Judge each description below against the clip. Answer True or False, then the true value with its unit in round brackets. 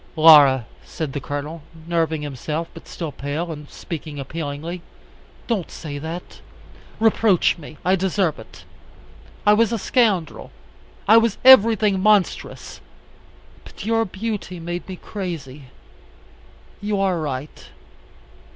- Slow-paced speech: True (120 wpm)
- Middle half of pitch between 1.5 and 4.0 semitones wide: False (5.2 semitones)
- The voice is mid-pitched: True (170 Hz)